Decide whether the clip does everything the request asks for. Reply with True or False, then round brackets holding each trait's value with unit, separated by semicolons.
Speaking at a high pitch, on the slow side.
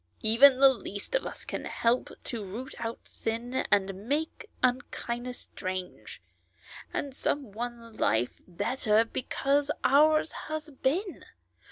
True (245 Hz; 130 wpm)